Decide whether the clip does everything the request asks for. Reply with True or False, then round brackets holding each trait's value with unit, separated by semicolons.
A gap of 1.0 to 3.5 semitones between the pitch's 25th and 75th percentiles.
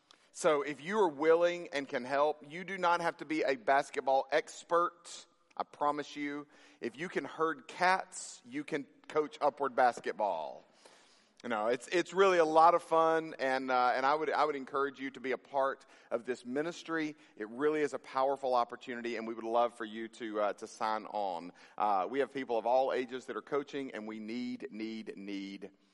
False (4.6 semitones)